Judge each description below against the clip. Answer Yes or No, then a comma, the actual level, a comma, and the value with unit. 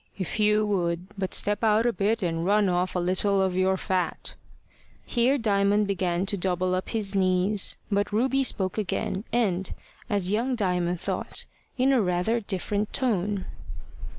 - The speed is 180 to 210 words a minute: No, average, 160 wpm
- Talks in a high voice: Yes, high, 200 Hz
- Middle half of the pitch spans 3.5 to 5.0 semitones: No, narrow, 2.6 semitones